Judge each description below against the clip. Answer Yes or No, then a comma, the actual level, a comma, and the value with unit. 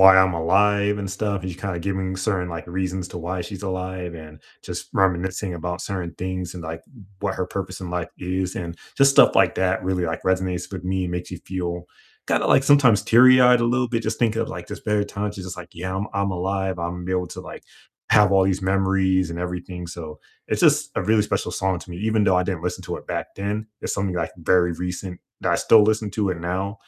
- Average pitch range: No, narrow, 2.1 semitones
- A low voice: Yes, very low, 95 Hz